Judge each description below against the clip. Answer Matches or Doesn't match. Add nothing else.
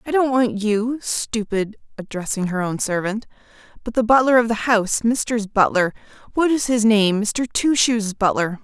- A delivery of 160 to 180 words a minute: Matches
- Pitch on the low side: Doesn't match